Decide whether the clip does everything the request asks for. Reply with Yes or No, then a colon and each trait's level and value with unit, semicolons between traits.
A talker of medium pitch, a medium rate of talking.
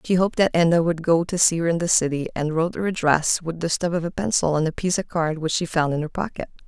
No: medium, 170 Hz; fast, 295 wpm